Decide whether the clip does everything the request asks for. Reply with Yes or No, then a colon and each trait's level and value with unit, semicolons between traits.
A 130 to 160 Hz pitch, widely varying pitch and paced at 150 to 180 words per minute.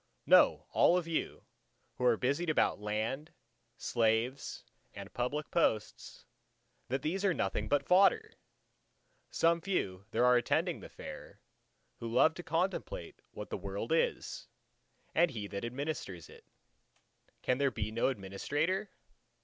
No: low, 135 Hz; wide, 7.2 semitones; slow, 135 wpm